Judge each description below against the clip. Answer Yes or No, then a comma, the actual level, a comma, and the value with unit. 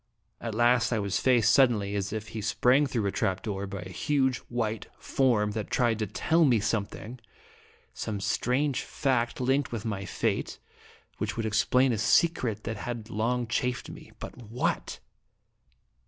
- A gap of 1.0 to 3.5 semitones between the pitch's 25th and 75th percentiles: Yes, average, 3.1 semitones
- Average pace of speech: Yes, average, 165 wpm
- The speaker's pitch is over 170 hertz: No, low, 115 Hz